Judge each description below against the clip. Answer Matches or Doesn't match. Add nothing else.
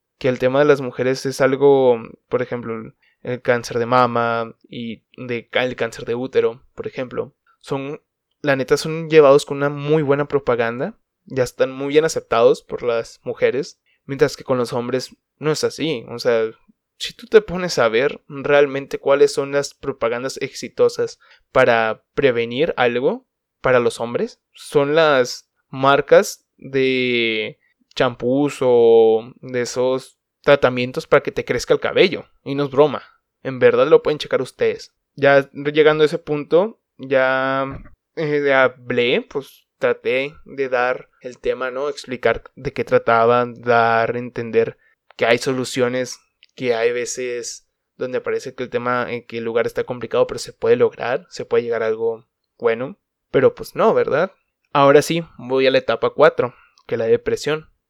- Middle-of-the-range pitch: Matches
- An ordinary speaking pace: Matches